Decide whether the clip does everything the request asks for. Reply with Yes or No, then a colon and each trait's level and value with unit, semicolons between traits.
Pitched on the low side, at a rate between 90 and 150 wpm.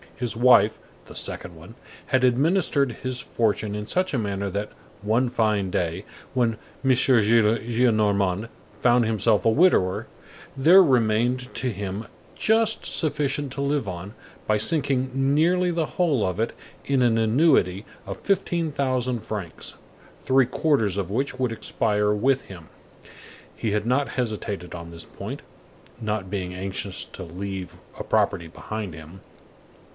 Yes: low, 115 Hz; average, 140 wpm